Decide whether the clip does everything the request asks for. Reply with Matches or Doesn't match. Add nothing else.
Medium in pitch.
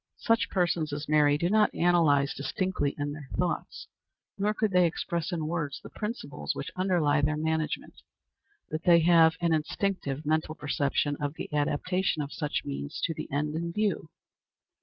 Matches